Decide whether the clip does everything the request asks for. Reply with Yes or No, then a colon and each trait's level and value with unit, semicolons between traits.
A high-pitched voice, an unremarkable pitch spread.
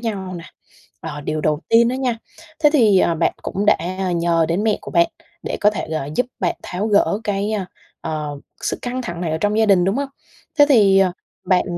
Yes: high, 195 Hz; average, 4.3 semitones